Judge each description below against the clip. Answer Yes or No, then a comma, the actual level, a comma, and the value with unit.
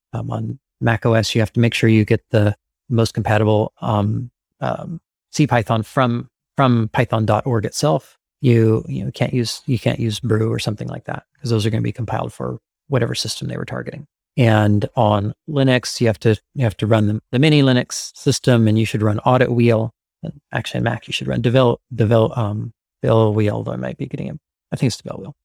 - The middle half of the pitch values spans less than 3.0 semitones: Yes, narrow, 2.4 semitones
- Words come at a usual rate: No, fast, 210 wpm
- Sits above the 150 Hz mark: No, low, 115 Hz